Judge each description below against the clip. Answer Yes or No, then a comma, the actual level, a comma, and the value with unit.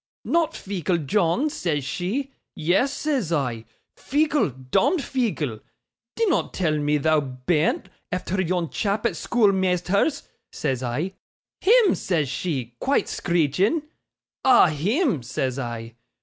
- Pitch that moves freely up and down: Yes, wide, 8.7 semitones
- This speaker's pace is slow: Yes, slow, 120 wpm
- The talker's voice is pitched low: No, medium, 180 Hz